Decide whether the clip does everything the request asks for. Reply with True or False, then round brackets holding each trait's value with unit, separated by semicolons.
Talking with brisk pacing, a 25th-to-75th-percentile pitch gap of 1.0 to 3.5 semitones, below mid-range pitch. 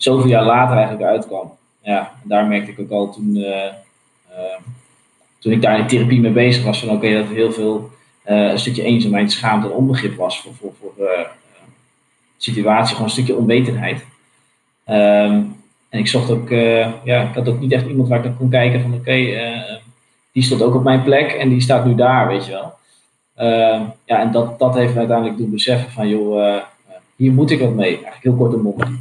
True (220 wpm; 2.7 semitones; 120 Hz)